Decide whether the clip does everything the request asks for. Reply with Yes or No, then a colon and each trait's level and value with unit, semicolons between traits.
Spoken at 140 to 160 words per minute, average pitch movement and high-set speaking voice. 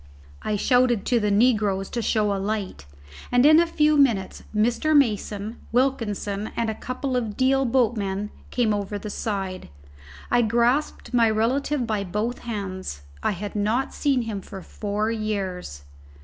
Yes: average, 155 wpm; average, 3.5 semitones; high, 220 Hz